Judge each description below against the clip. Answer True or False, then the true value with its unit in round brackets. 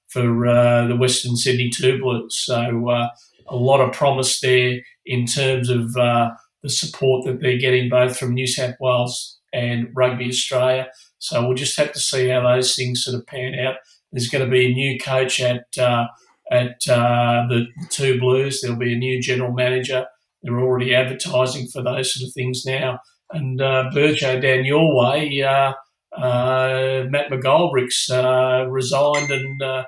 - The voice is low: True (130 Hz)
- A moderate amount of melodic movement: False (1.1 semitones)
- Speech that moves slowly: False (175 wpm)